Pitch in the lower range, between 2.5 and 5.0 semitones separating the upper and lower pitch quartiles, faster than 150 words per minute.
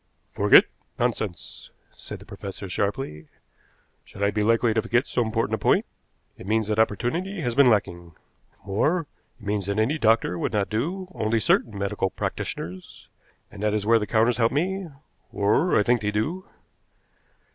Yes: low, 110 Hz; average, 3.2 semitones; average, 170 wpm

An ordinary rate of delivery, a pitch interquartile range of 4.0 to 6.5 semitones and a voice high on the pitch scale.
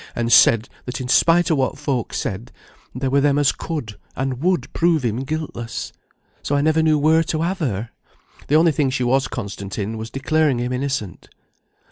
No: average, 190 wpm; average, 4.7 semitones; low, 135 Hz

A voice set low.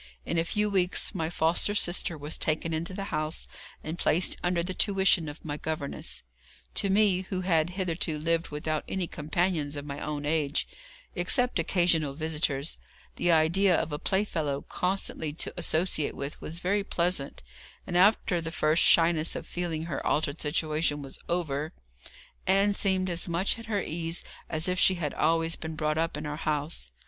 No: medium, 165 Hz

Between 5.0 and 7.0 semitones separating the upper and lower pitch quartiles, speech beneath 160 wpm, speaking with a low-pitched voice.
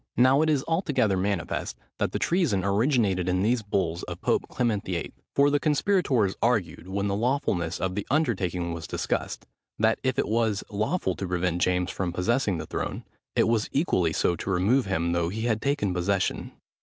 No: wide, 5.6 semitones; average, 185 wpm; low, 100 Hz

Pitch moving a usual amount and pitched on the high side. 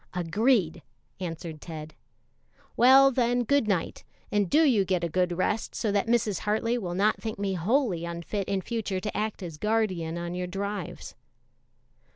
Yes: average, 4.4 semitones; high, 200 Hz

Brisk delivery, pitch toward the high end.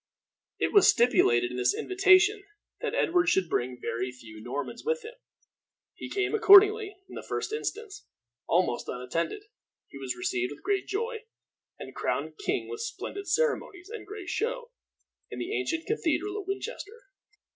No: average, 155 wpm; very high, 390 Hz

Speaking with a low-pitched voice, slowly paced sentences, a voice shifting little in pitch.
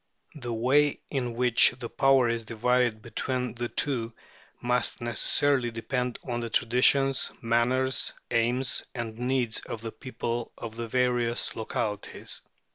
Yes: low, 120 Hz; slow, 130 wpm; narrow, 1.7 semitones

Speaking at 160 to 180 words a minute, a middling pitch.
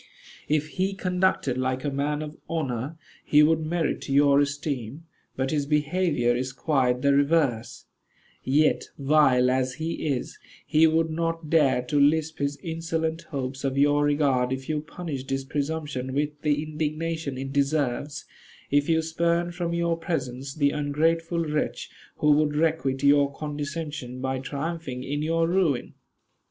No: average, 150 wpm; medium, 150 Hz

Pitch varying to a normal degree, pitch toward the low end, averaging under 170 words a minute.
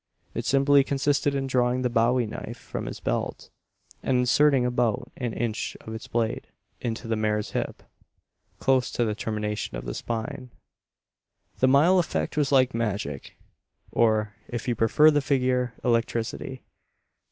Yes: average, 3.0 semitones; low, 125 Hz; average, 145 wpm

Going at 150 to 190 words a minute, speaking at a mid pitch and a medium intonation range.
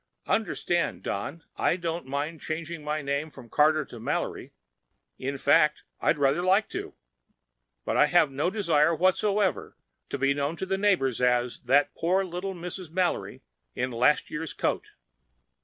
Yes: average, 155 wpm; medium, 155 Hz; average, 4.2 semitones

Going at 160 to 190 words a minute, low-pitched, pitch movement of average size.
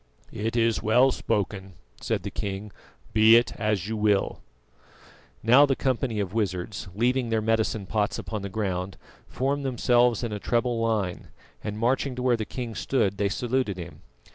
Yes: average, 165 wpm; low, 110 Hz; average, 3.2 semitones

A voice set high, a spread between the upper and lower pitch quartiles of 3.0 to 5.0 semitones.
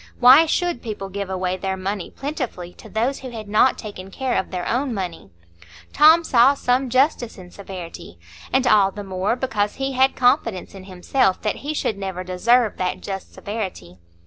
No: high, 210 Hz; wide, 5.4 semitones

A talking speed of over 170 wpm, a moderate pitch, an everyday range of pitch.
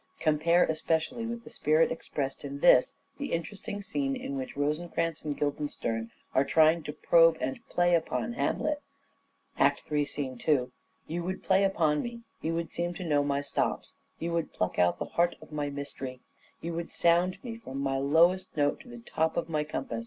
Yes: average, 180 wpm; medium, 165 Hz; average, 4.1 semitones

